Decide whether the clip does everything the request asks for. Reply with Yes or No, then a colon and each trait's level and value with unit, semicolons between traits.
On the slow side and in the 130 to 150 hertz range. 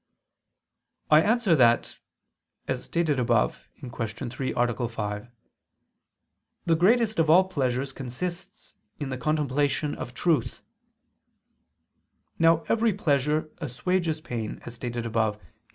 Yes: slow, 115 wpm; medium, 140 Hz